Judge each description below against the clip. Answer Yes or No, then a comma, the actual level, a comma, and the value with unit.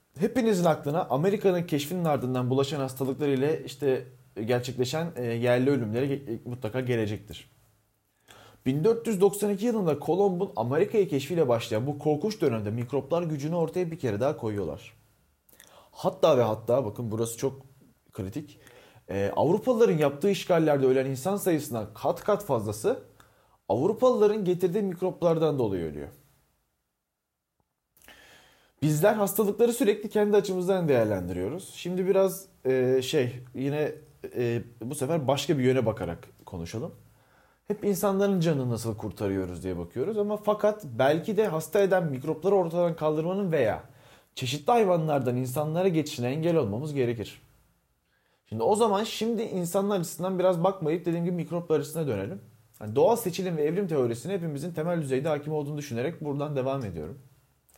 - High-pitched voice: No, medium, 150 Hz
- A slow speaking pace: No, average, 125 wpm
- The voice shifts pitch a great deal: Yes, wide, 6.9 semitones